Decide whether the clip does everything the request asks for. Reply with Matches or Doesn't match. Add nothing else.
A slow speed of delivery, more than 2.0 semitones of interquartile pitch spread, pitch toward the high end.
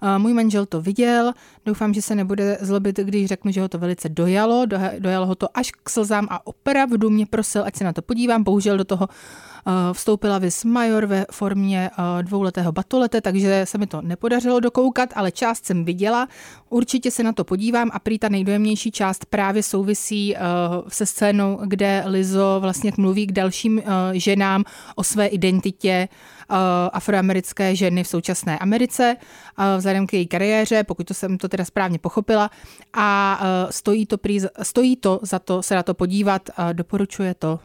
Doesn't match